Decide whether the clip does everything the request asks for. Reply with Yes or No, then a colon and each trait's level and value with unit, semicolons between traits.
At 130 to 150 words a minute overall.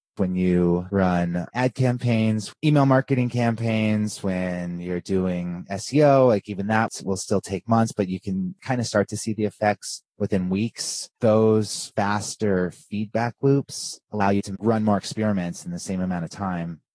No: average, 165 wpm